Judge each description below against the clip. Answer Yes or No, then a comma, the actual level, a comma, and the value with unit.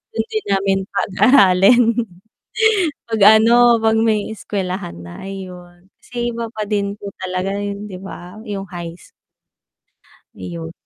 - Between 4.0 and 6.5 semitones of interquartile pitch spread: No, average, 3.3 semitones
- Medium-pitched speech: No, high, 200 Hz